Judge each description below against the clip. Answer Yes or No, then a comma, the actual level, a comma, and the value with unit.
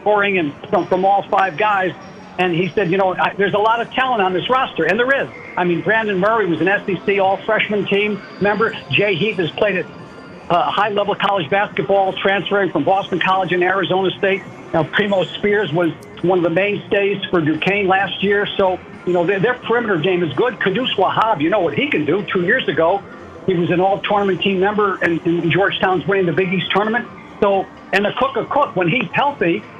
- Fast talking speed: Yes, fast, 215 wpm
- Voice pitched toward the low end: No, high, 195 Hz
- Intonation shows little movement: Yes, narrow, 1.8 semitones